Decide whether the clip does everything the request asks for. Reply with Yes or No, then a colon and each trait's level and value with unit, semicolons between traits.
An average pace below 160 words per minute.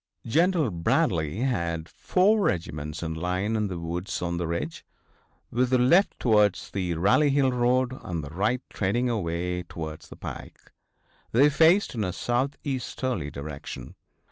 Yes: average, 145 wpm